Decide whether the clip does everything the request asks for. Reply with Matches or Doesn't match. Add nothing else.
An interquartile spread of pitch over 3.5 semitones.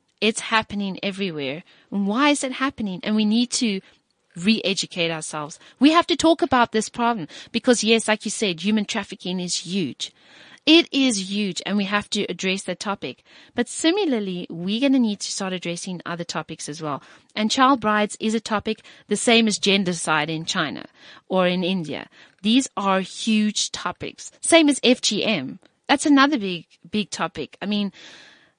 Matches